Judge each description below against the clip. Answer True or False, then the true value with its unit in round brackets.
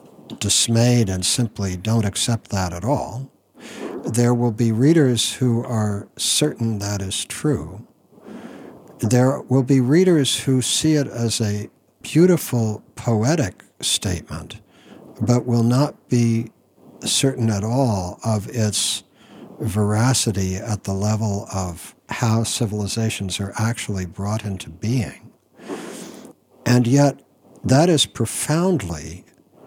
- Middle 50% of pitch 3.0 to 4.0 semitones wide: True (3.6 semitones)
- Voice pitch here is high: False (115 Hz)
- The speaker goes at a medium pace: False (115 wpm)